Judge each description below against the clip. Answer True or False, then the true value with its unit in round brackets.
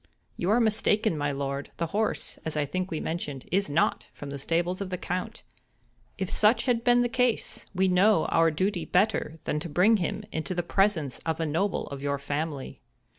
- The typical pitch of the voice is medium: True (175 Hz)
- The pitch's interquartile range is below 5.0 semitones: False (5.3 semitones)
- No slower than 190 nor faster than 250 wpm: True (200 wpm)